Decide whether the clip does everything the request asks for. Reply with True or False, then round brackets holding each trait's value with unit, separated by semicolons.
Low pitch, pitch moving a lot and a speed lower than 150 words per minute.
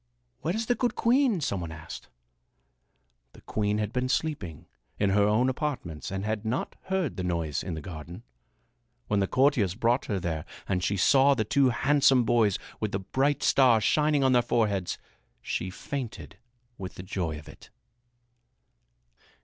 False (110 Hz; 6.5 semitones; 165 wpm)